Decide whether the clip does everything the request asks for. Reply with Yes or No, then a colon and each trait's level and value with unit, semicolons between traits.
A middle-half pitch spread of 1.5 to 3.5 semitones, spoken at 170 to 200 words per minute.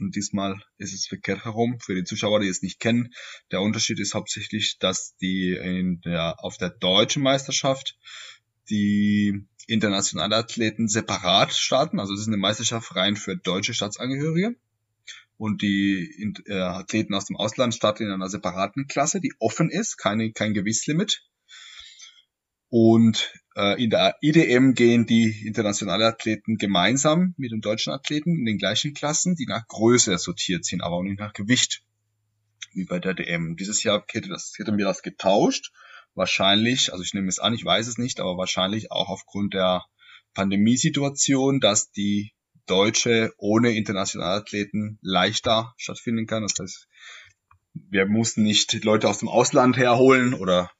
No: average, 3.1 semitones; average, 160 wpm